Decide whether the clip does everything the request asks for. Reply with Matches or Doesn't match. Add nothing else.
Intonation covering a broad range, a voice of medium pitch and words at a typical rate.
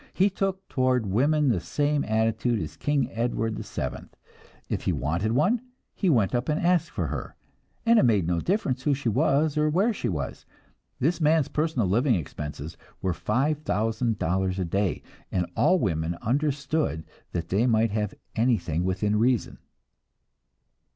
Doesn't match